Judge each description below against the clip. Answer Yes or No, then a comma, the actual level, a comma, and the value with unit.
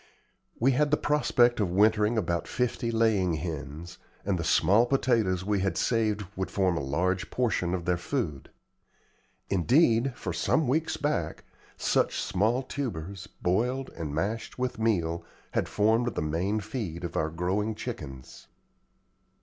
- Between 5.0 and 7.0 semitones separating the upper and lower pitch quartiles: Yes, wide, 5.6 semitones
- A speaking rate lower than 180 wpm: Yes, average, 145 wpm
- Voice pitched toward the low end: Yes, low, 105 Hz